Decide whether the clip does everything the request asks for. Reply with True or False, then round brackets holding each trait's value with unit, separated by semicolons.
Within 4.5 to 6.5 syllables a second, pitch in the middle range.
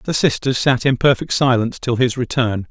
False (5.2 syllables/s; 125 Hz)